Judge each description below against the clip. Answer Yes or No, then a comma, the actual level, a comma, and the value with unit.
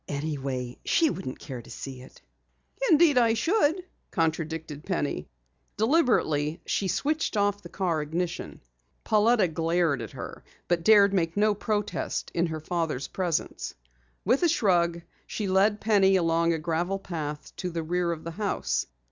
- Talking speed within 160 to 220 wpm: No, average, 150 wpm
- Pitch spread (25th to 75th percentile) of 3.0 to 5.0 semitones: Yes, average, 4.6 semitones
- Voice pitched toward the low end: No, medium, 175 Hz